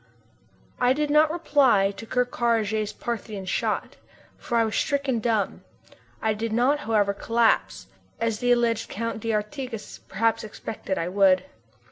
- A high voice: Yes, high, 225 Hz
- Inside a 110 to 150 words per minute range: Yes, average, 140 wpm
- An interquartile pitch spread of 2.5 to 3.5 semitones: Yes, average, 2.8 semitones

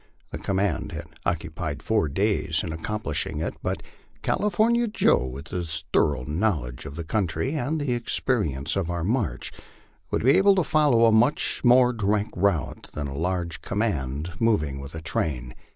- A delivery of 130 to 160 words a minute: No, average, 170 wpm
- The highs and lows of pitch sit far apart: Yes, wide, 6.9 semitones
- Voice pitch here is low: Yes, very low, 90 Hz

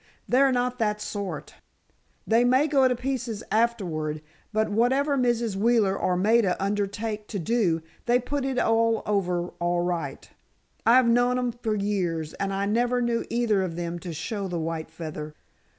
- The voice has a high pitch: Yes, high, 215 Hz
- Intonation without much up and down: No, average, 5.1 semitones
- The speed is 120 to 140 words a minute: No, average, 160 wpm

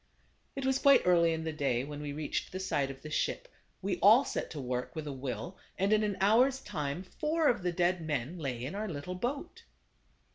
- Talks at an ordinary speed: No, fast, 220 wpm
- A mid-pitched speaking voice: Yes, medium, 175 Hz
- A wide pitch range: Yes, wide, 6.6 semitones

